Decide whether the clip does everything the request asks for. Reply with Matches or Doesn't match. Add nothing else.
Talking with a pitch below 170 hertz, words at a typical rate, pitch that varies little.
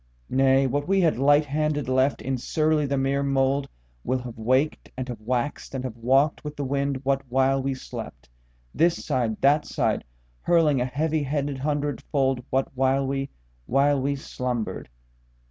Matches